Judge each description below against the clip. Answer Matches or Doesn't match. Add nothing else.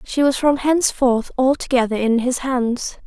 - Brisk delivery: Doesn't match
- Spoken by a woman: Matches